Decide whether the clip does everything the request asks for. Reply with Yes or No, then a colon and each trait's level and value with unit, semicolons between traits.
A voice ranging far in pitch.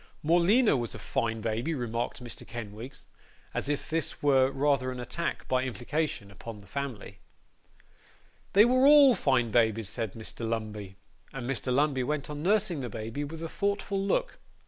Yes: wide, 5.8 semitones